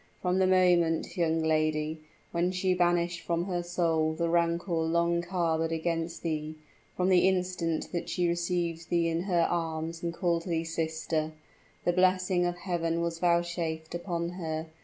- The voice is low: No, medium, 170 Hz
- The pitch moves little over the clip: Yes, narrow, 1.4 semitones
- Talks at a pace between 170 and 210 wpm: No, average, 160 wpm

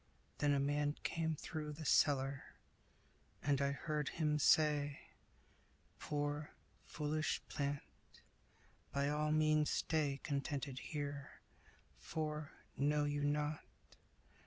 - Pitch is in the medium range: Yes, medium, 145 Hz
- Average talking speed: No, slow, 105 wpm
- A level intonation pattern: Yes, narrow, 1.2 semitones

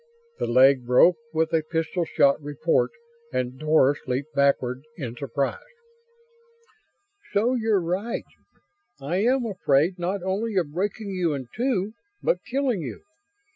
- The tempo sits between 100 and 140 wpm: Yes, slow, 135 wpm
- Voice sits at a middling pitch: Yes, medium, 170 Hz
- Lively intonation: Yes, wide, 6.6 semitones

